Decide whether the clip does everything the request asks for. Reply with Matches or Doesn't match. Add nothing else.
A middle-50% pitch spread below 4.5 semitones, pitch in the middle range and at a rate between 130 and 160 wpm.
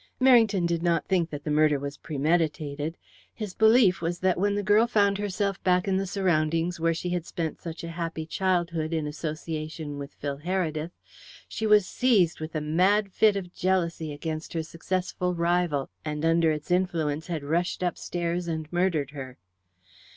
Doesn't match